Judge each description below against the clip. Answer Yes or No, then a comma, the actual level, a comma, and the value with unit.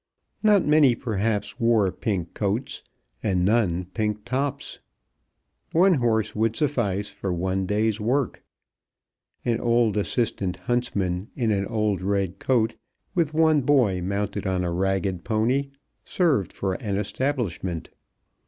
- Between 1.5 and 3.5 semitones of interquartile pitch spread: No, average, 4.3 semitones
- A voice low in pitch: Yes, low, 105 Hz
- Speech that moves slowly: Yes, slow, 125 wpm